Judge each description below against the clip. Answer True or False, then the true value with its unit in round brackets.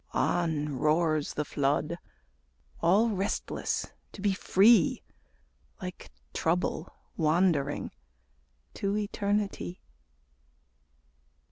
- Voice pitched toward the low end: False (170 Hz)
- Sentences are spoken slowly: True (75 wpm)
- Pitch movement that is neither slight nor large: True (4.6 semitones)